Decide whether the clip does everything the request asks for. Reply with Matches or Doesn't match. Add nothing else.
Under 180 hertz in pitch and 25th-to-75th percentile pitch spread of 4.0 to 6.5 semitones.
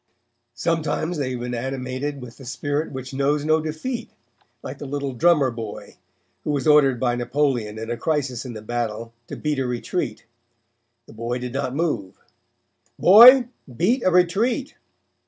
Matches